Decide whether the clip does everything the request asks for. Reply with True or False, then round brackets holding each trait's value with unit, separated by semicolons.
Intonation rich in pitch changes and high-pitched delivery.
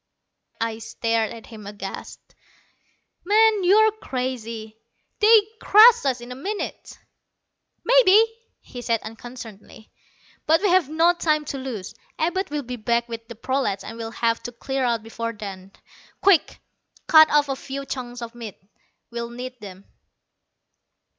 True (5.7 semitones; 245 Hz)